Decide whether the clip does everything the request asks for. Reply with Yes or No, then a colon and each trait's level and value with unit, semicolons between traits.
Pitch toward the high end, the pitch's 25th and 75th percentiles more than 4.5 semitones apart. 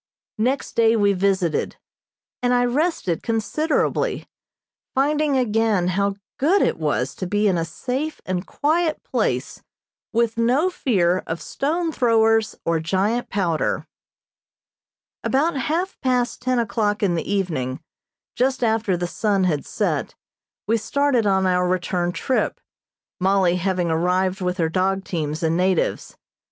Yes: high, 205 Hz; wide, 5.6 semitones